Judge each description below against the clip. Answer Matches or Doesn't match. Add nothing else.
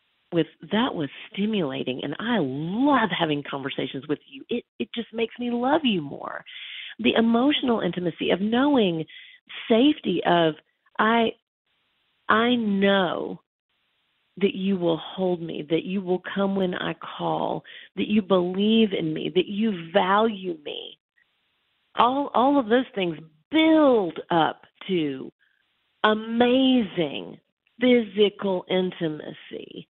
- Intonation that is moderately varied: Doesn't match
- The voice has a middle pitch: Doesn't match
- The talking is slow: Matches